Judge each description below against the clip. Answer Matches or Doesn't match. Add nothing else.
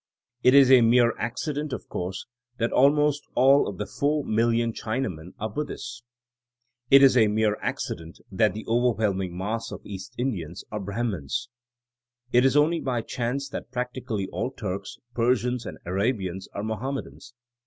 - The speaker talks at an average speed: Matches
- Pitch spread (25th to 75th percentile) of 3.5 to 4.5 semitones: Matches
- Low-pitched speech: Matches